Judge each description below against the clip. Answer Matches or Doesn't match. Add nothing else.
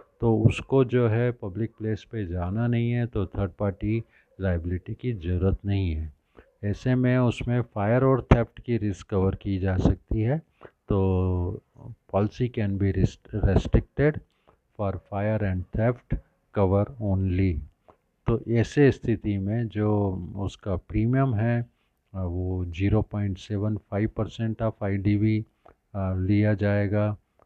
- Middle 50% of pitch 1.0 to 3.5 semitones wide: Matches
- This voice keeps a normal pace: Matches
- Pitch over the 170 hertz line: Doesn't match